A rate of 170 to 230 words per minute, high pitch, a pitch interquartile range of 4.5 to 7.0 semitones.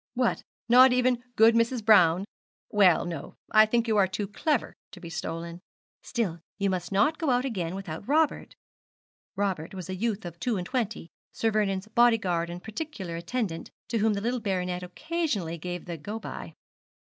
Yes: average, 180 wpm; high, 205 Hz; average, 4.8 semitones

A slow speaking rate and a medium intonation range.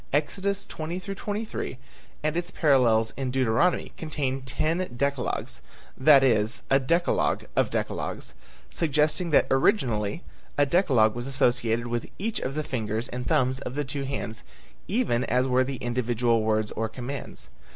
No: average, 145 wpm; average, 4.4 semitones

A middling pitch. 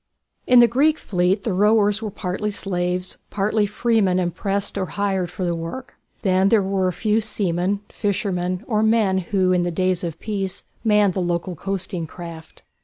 No: high, 195 Hz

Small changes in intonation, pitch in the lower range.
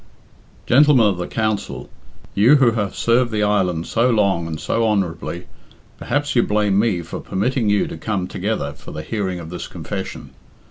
No: average, 4.3 semitones; low, 105 Hz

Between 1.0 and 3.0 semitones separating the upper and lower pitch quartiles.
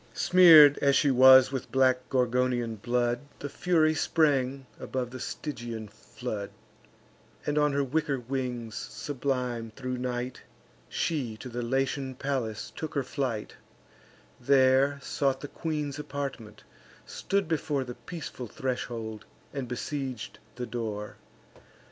Yes: average, 2.7 semitones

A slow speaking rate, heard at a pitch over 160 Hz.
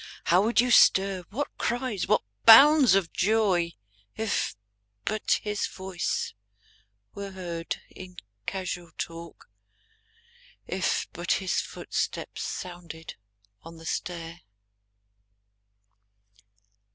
Yes: slow, 95 wpm; medium, 185 Hz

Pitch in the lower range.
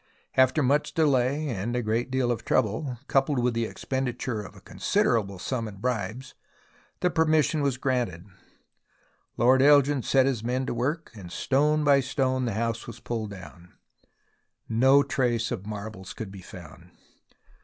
Yes: low, 125 Hz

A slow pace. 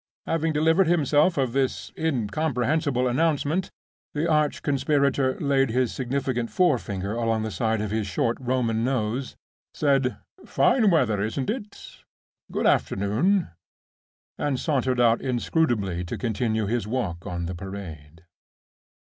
Yes: slow, 125 wpm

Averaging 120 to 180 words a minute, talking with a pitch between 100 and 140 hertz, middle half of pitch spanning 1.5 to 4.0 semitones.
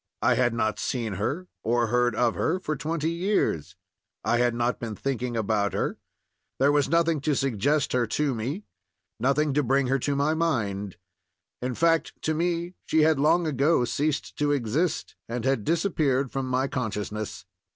No: average, 170 wpm; low, 135 Hz; average, 4.6 semitones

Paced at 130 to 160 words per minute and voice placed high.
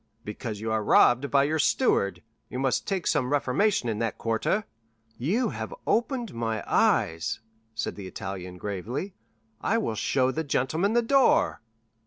No: average, 155 wpm; low, 130 Hz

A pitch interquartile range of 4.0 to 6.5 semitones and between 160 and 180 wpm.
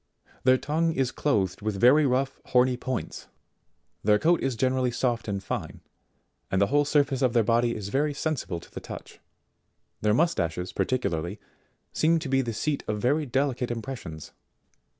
Yes: average, 4.8 semitones; average, 165 wpm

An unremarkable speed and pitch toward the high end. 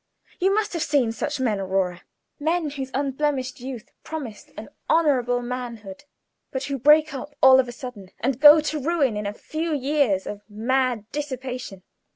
Yes: average, 170 wpm; very high, 260 Hz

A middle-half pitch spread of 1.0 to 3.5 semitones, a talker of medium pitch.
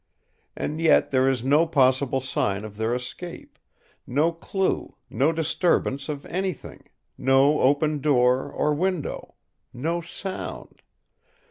No: average, 4.0 semitones; medium, 145 Hz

